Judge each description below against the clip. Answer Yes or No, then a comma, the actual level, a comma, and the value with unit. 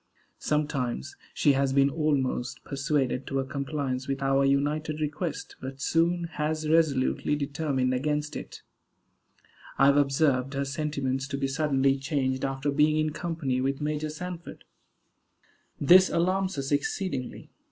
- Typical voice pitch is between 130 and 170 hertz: Yes, medium, 140 Hz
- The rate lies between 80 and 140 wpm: Yes, slow, 135 wpm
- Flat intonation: Yes, narrow, 2.2 semitones